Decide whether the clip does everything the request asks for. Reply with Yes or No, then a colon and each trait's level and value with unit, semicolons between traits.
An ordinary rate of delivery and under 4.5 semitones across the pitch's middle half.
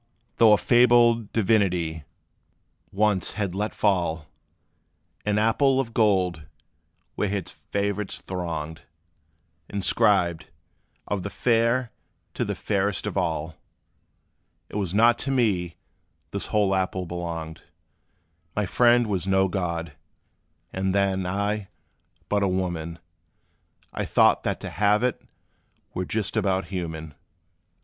No: slow, 120 wpm; average, 3.3 semitones